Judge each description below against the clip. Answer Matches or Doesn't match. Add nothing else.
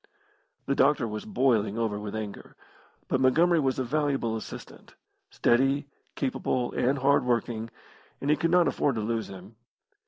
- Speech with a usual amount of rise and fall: Matches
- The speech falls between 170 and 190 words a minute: Doesn't match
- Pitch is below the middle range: Matches